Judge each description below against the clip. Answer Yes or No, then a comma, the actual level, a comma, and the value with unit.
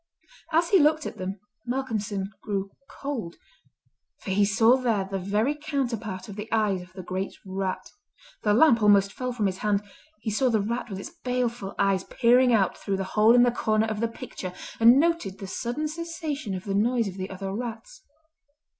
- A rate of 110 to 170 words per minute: No, average, 190 wpm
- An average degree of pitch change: Yes, average, 4.2 semitones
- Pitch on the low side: No, high, 215 Hz